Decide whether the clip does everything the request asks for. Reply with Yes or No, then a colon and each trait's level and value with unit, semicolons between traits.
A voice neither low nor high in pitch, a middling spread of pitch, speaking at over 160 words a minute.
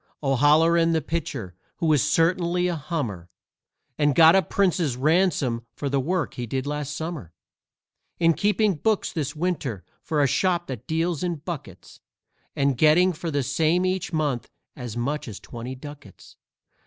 No: medium, 150 Hz; average, 4.2 semitones; average, 155 wpm